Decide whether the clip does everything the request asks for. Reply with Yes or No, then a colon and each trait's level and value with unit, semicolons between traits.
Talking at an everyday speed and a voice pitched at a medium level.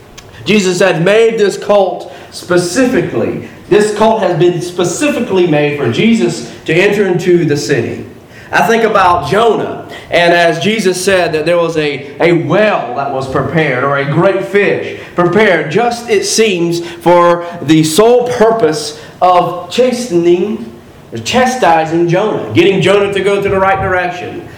Yes: average, 150 wpm; medium, 175 Hz